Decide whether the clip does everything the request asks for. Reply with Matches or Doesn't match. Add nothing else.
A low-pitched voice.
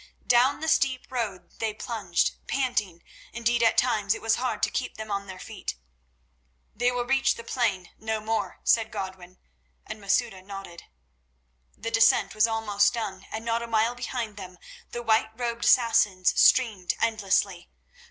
Doesn't match